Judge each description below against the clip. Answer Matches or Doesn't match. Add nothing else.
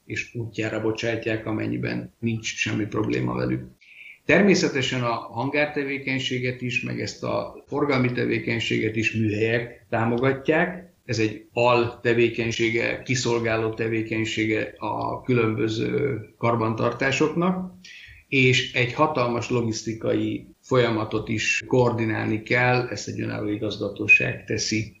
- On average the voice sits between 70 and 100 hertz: Doesn't match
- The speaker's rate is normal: Doesn't match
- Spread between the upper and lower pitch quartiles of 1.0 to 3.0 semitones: Matches